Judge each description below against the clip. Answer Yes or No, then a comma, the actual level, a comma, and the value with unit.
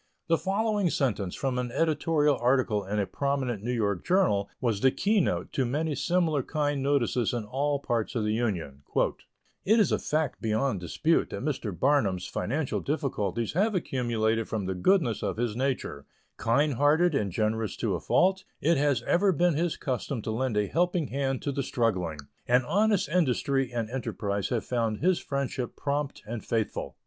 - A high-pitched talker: No, low, 130 Hz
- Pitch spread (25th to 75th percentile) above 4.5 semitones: Yes, wide, 5.5 semitones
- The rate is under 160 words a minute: No, average, 175 wpm